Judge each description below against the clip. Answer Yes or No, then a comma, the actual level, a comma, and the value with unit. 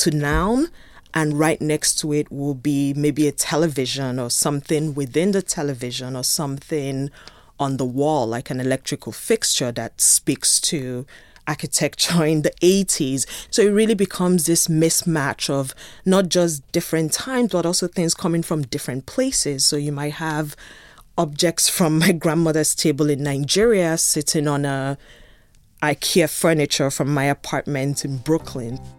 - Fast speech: No, average, 150 wpm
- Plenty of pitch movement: No, average, 3.3 semitones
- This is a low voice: No, medium, 150 Hz